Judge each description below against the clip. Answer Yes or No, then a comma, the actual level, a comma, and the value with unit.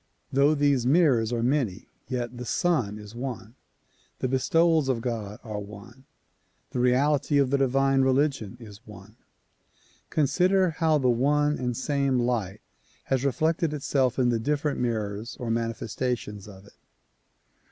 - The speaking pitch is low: Yes, low, 125 Hz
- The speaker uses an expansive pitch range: No, average, 3.9 semitones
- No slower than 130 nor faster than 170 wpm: Yes, average, 140 wpm